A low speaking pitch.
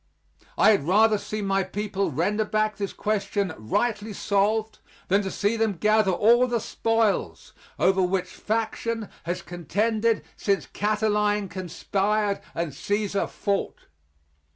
No: high, 205 Hz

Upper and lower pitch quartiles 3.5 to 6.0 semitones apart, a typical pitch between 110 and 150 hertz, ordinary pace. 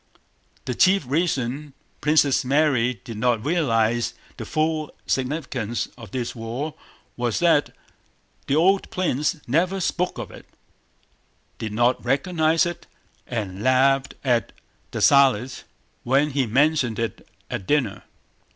No: average, 4.5 semitones; low, 135 Hz; slow, 120 wpm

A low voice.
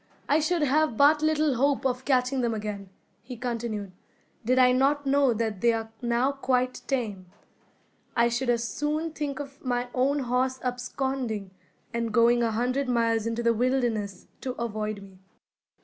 No: very high, 250 Hz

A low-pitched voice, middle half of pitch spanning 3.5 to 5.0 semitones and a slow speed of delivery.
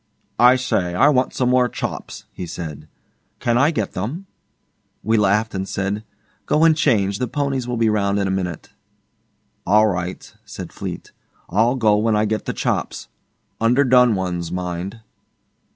No: low, 110 Hz; average, 4.6 semitones; average, 160 wpm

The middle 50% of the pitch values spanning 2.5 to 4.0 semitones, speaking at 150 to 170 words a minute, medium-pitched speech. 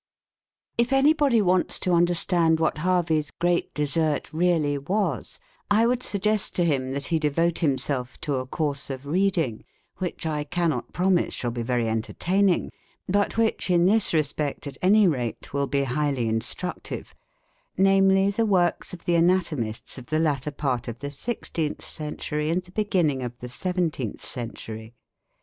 No: average, 4.9 semitones; average, 155 wpm; medium, 160 Hz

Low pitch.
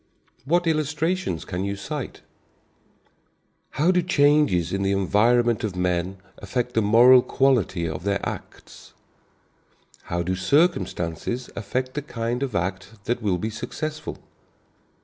Yes: low, 115 Hz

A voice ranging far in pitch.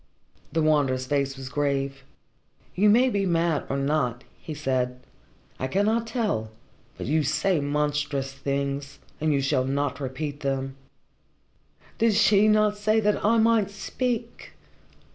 Yes: wide, 7.1 semitones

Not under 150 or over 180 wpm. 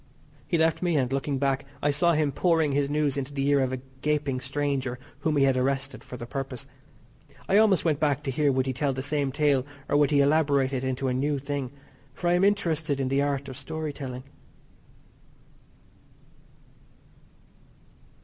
No: average, 190 wpm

